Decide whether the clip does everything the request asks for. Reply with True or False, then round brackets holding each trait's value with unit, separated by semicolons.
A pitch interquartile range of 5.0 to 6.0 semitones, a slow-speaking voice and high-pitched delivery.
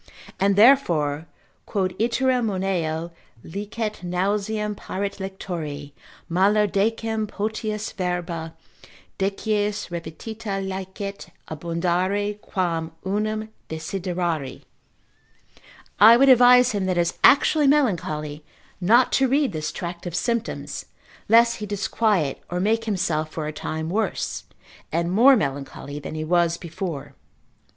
False (4.3 semitones; 110 wpm; 195 Hz)